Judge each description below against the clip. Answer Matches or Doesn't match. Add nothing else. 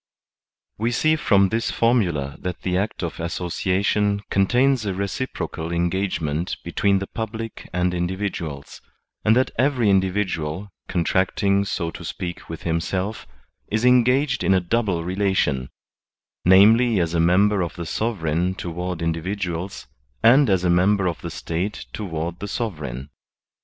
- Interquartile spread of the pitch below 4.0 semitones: Matches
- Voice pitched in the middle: Doesn't match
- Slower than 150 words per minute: Matches